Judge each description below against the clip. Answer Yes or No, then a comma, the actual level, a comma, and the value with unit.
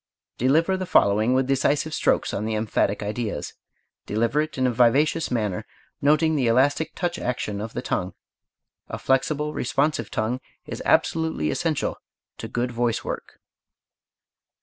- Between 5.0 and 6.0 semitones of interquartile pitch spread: Yes, average, 5.3 semitones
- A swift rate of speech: No, average, 145 wpm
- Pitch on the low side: Yes, low, 125 Hz